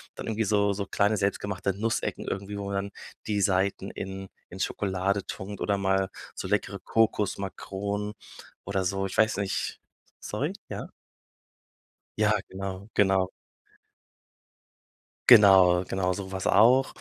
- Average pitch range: No, narrow, 1.2 semitones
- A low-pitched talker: Yes, low, 100 Hz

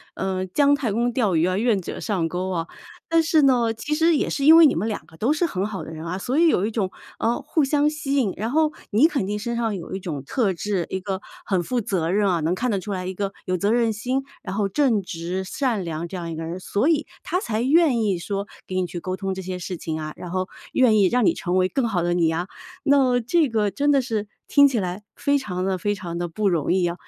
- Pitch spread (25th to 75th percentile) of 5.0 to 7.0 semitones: Yes, wide, 5.6 semitones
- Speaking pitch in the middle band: No, high, 205 Hz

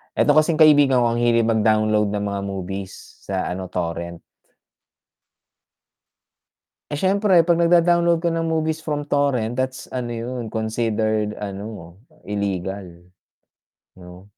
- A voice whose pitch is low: Yes, low, 115 Hz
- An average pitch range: No, wide, 7.0 semitones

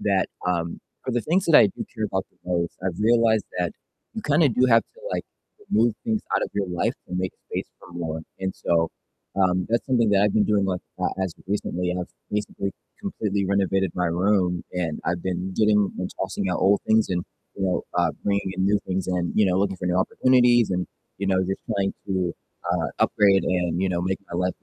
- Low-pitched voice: Yes, very low, 95 Hz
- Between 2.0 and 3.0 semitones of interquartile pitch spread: Yes, average, 2.7 semitones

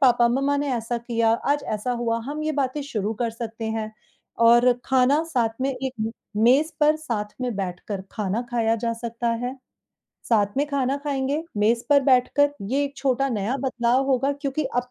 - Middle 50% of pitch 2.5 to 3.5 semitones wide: Yes, average, 3.2 semitones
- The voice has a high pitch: Yes, very high, 250 Hz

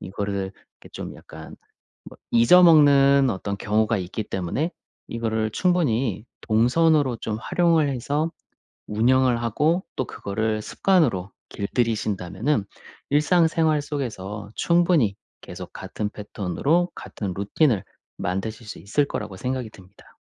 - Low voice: Yes, low, 115 Hz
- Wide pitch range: Yes, wide, 6.2 semitones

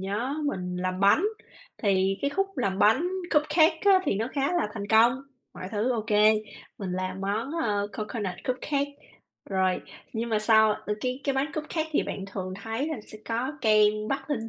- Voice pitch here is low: No, high, 225 Hz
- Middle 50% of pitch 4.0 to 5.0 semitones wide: No, wide, 5.5 semitones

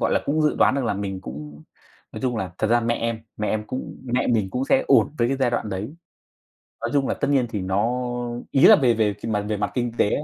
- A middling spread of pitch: Yes, average, 3.9 semitones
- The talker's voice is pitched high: No, low, 115 Hz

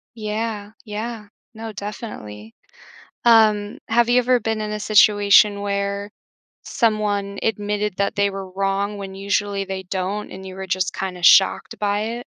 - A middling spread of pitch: No, narrow, 1.5 semitones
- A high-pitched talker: Yes, high, 205 Hz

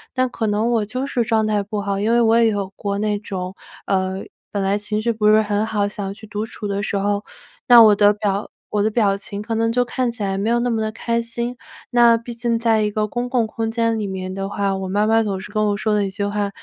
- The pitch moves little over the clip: Yes, narrow, 2.2 semitones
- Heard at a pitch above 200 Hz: Yes, high, 215 Hz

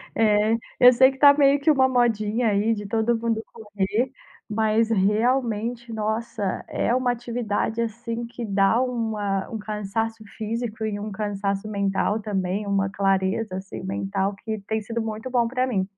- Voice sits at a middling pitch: No, high, 220 Hz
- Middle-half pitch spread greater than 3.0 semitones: No, narrow, 2.5 semitones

